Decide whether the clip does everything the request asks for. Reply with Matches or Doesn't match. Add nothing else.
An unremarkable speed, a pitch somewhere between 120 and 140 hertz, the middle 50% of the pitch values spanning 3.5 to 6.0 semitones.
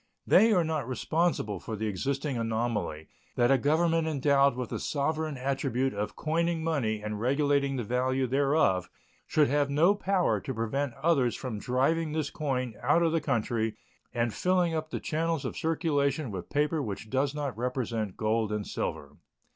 Matches